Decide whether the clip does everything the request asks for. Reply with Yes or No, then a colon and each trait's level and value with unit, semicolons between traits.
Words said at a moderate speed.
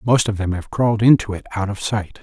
No: fast, 270 wpm